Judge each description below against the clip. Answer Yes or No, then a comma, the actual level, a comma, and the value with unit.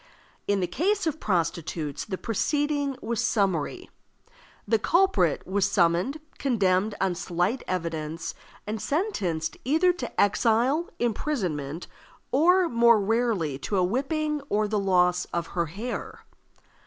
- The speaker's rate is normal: No, slow, 125 wpm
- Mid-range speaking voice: No, high, 210 Hz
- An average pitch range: No, wide, 7.7 semitones